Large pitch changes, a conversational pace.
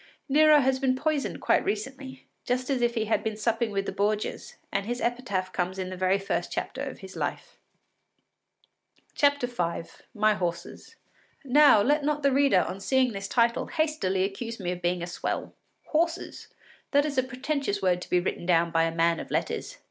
Yes: wide, 6.3 semitones; average, 185 wpm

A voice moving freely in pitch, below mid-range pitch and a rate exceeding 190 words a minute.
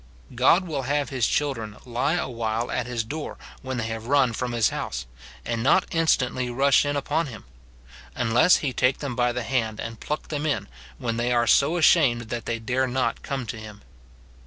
No: average, 3.3 semitones; low, 125 Hz; average, 200 wpm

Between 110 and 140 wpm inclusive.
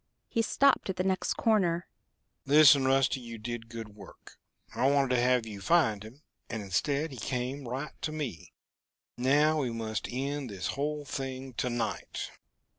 No: average, 165 wpm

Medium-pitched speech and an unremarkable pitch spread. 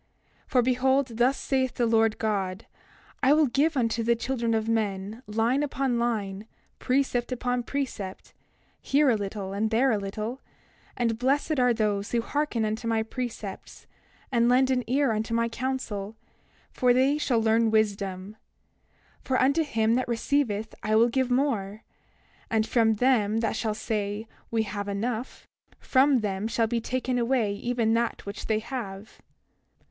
No: high, 230 Hz; average, 3.0 semitones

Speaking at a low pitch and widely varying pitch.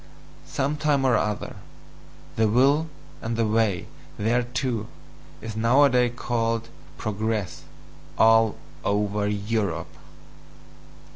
No: low, 115 Hz; average, 2.8 semitones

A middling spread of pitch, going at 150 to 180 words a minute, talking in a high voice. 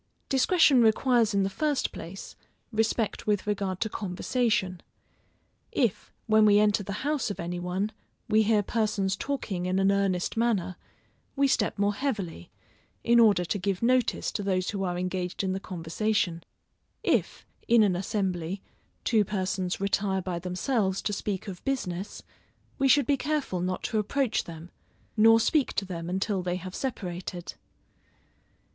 Yes: average, 3.6 semitones; average, 155 wpm; high, 200 Hz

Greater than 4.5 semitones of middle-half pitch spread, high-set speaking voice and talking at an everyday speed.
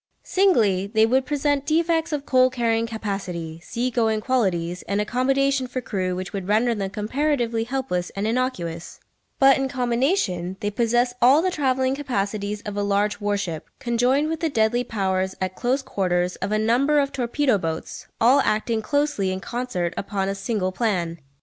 Yes: average, 5.0 semitones; high, 225 Hz; average, 170 wpm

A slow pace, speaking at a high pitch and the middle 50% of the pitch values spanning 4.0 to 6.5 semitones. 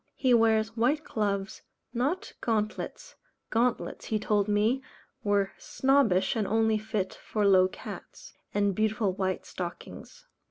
No: slow, 125 wpm; high, 215 Hz; average, 2.8 semitones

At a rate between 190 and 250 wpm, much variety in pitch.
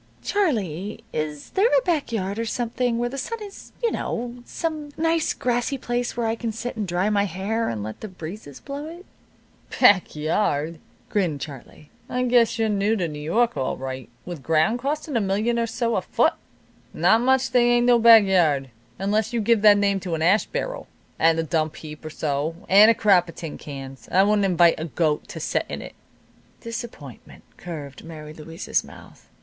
Yes: average, 195 wpm; wide, 6.9 semitones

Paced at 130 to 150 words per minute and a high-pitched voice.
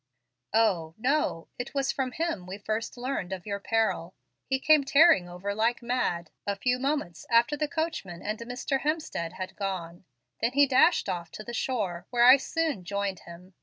No: average, 180 wpm; high, 225 Hz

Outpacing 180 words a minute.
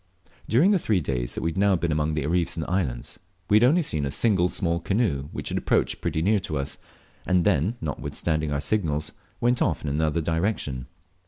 Yes: average, 200 wpm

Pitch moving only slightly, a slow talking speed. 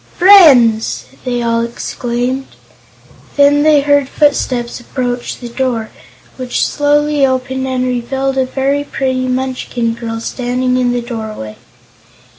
Yes: narrow, 2.1 semitones; slow, 120 wpm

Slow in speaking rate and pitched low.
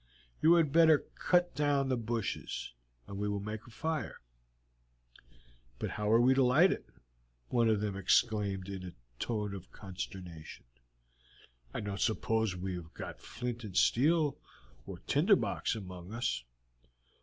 No: average, 150 wpm; low, 110 Hz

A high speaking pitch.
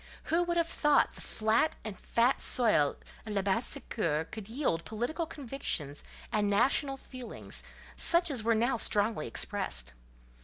Yes: high, 230 Hz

